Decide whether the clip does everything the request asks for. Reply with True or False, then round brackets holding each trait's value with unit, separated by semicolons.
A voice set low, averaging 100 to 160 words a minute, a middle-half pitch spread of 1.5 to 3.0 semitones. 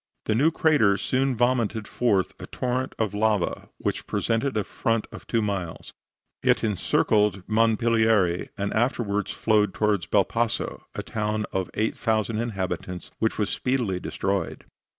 True (110 Hz; 135 wpm; 2.5 semitones)